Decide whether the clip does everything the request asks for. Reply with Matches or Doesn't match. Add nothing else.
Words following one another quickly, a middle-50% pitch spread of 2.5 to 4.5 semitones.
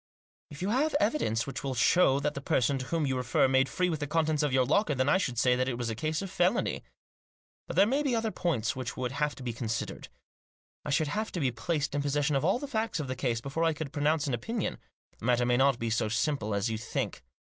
Doesn't match